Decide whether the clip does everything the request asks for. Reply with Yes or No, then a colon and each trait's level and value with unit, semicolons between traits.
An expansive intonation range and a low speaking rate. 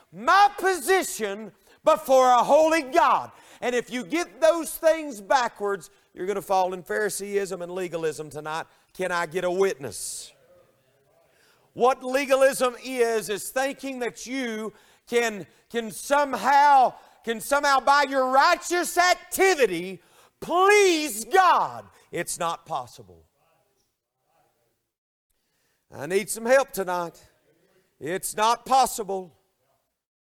Yes: wide, 7.2 semitones; slow, 110 wpm